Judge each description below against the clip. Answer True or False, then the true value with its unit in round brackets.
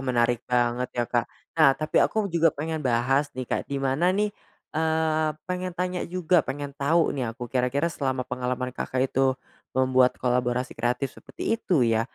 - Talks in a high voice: False (135 Hz)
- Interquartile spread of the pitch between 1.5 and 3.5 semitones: False (4.1 semitones)